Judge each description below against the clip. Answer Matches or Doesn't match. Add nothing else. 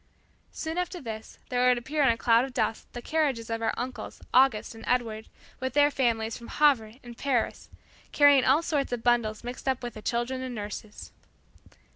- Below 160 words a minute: Doesn't match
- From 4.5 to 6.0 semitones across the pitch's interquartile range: Doesn't match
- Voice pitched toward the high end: Matches